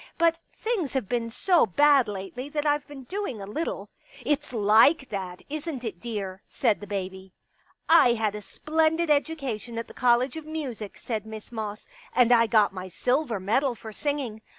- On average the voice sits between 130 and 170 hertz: No, high, 240 Hz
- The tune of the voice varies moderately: No, wide, 5.7 semitones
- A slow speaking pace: No, average, 195 wpm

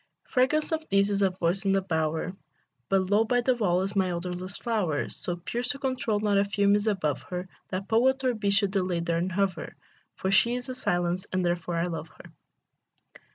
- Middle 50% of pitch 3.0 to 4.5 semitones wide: Yes, average, 3.8 semitones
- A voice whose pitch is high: Yes, high, 195 Hz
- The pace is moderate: No, fast, 210 wpm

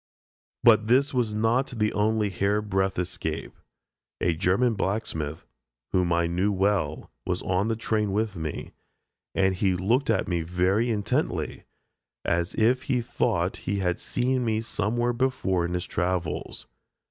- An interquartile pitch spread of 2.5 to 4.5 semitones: Yes, average, 4.0 semitones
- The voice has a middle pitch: No, low, 100 Hz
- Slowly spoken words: No, average, 145 wpm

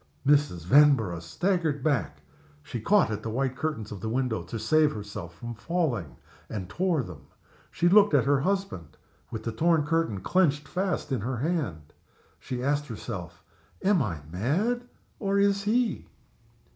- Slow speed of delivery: No, average, 160 wpm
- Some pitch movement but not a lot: No, wide, 8.3 semitones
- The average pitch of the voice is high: No, low, 135 Hz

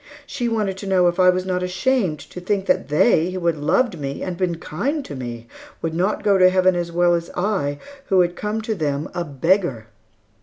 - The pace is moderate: No, fast, 220 wpm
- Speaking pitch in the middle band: Yes, medium, 180 Hz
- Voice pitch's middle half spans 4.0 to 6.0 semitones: No, average, 3.2 semitones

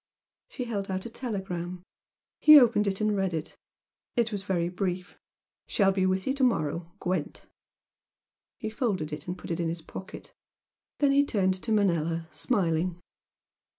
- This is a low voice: No, high, 190 Hz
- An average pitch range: Yes, average, 4.0 semitones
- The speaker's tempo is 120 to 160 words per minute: Yes, average, 155 wpm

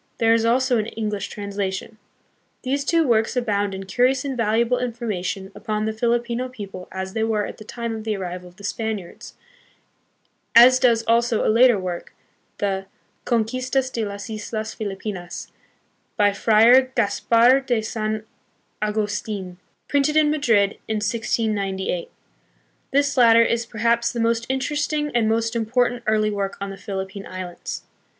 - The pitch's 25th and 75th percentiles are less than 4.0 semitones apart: Yes, average, 2.9 semitones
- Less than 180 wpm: Yes, average, 150 wpm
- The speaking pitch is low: No, high, 220 Hz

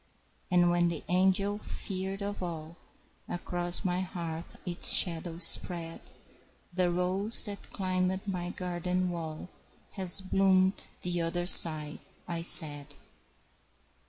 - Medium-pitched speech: Yes, medium, 180 Hz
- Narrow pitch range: Yes, narrow, 1.6 semitones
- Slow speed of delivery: Yes, slow, 115 wpm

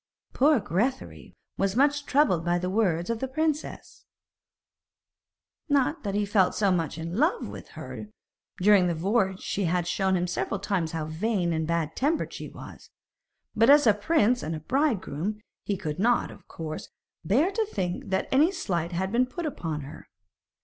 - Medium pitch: No, high, 195 Hz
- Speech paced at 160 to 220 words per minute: Yes, average, 180 wpm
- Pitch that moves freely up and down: Yes, wide, 6.9 semitones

